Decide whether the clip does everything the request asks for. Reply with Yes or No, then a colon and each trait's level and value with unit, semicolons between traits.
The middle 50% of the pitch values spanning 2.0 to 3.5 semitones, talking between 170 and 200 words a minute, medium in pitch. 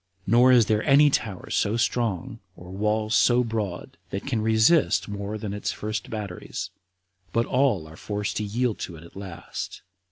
No: average, 2.8 semitones; average, 180 wpm; low, 110 Hz